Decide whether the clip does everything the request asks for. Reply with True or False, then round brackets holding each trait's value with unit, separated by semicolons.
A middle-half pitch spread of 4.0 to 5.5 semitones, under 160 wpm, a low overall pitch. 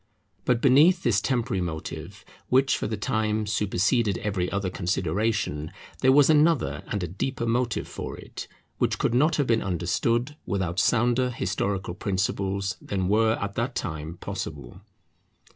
True (4.7 semitones; 145 wpm; 105 Hz)